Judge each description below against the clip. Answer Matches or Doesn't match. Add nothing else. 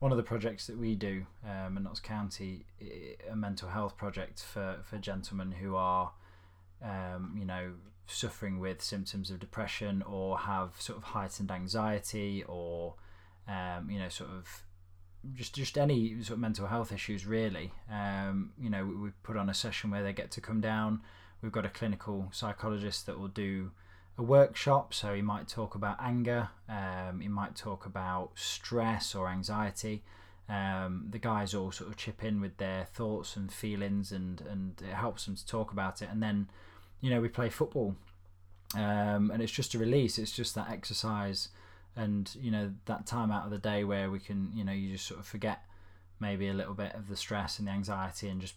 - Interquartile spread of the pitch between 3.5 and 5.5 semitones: Doesn't match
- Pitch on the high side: Doesn't match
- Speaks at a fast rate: Doesn't match